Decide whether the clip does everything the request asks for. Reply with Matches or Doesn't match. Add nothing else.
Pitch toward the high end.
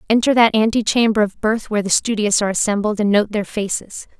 Matches